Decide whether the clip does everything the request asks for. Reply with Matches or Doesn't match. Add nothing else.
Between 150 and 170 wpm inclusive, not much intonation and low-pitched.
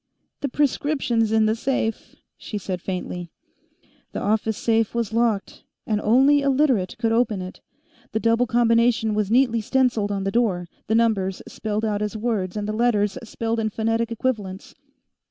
Doesn't match